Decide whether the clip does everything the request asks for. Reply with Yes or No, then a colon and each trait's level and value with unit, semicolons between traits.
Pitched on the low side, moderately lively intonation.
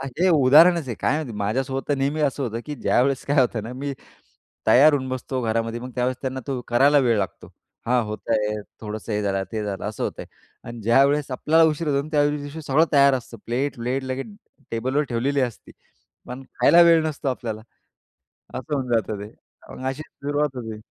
Yes: low, 130 Hz; average, 3.7 semitones